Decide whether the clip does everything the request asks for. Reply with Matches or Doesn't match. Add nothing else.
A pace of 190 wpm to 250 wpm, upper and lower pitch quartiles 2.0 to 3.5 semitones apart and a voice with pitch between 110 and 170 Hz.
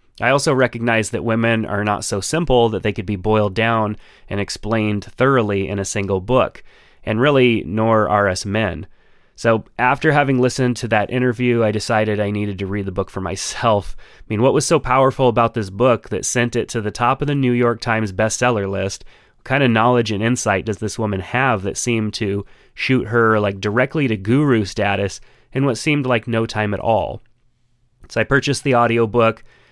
Matches